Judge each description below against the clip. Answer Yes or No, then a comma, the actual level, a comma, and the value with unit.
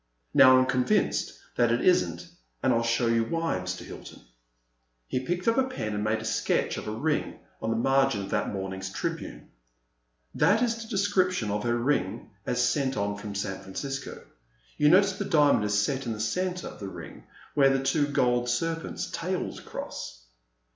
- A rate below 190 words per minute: No, average, 195 wpm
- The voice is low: Yes, low, 125 Hz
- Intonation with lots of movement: Yes, wide, 7.6 semitones